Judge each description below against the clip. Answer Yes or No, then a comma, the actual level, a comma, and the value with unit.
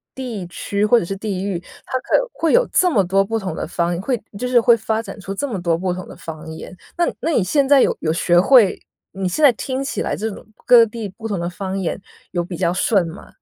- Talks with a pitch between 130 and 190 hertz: No, high, 200 Hz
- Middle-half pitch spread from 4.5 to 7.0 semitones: Yes, average, 4.9 semitones